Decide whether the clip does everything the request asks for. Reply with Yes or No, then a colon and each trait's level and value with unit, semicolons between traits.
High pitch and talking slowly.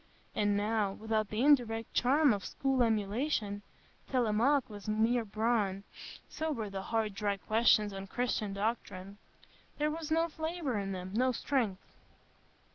Yes: high, 220 Hz; slow, 130 wpm